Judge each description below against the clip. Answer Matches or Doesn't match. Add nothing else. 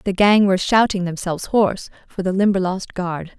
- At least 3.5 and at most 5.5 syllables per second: Matches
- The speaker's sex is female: Matches